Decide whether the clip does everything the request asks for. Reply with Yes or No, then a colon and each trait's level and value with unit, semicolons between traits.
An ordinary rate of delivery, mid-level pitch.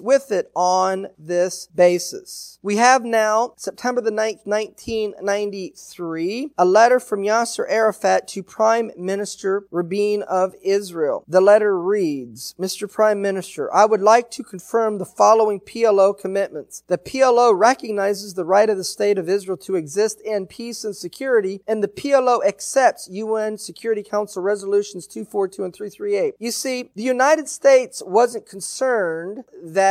No: average, 145 wpm; high, 205 Hz